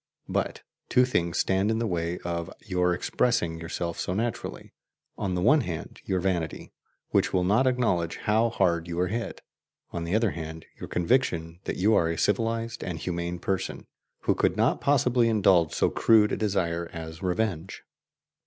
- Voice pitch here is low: Yes, very low, 90 Hz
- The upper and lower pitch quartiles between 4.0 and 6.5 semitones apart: Yes, average, 4.8 semitones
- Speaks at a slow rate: No, average, 170 wpm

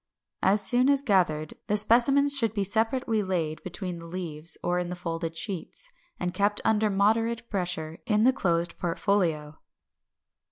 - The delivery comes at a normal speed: Yes, average, 155 wpm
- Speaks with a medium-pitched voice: No, high, 195 Hz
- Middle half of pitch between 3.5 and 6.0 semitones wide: Yes, average, 4.8 semitones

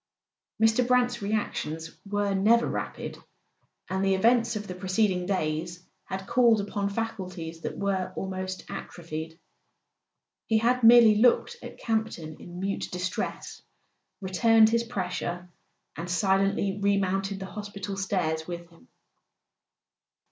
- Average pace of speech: No, slow, 120 wpm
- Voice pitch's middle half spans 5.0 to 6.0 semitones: No, average, 3.5 semitones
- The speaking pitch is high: Yes, high, 195 Hz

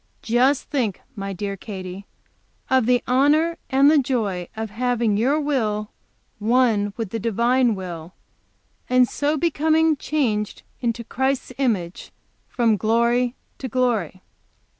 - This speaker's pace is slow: Yes, slow, 125 wpm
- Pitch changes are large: No, average, 4.0 semitones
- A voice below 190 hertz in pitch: No, high, 235 Hz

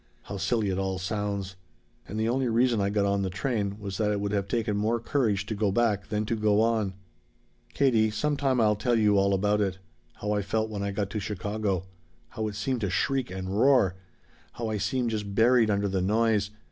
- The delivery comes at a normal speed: No, fast, 220 wpm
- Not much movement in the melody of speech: Yes, narrow, 2.3 semitones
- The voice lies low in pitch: Yes, low, 105 Hz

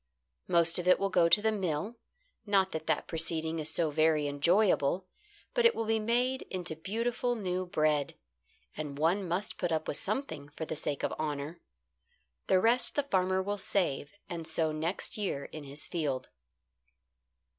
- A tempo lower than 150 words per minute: No, average, 170 wpm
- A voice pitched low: No, medium, 175 Hz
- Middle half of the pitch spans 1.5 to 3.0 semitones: No, average, 4.7 semitones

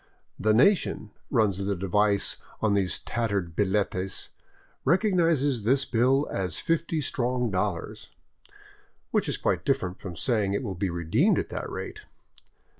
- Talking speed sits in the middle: Yes, average, 145 wpm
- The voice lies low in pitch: Yes, low, 110 Hz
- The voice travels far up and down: Yes, wide, 5.8 semitones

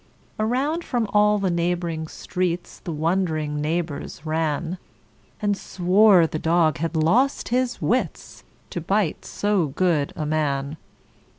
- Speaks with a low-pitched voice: No, medium, 175 Hz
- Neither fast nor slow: No, slow, 125 wpm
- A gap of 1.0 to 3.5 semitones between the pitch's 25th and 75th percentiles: No, average, 4.7 semitones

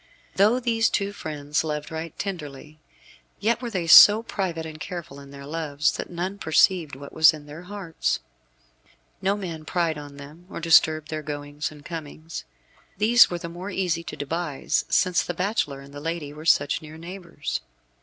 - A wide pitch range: No, average, 3.6 semitones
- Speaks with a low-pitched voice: No, medium, 165 Hz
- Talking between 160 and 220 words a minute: Yes, average, 175 wpm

